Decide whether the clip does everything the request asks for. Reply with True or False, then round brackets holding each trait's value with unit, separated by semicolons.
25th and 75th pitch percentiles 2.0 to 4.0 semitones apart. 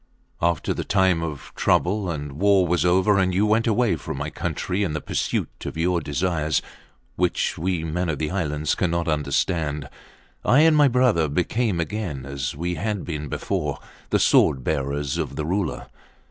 False (4.4 semitones)